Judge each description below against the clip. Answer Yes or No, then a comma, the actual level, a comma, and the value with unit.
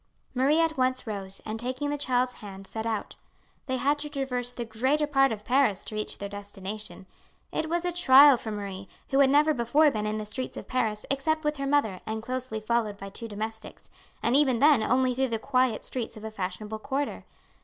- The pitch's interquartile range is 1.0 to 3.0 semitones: No, average, 4.3 semitones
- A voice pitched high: Yes, high, 245 Hz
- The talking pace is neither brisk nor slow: No, fast, 210 wpm